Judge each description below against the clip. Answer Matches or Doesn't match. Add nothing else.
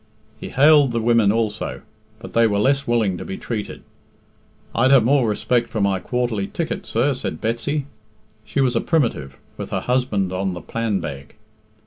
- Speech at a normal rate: Matches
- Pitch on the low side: Matches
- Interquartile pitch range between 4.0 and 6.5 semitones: Matches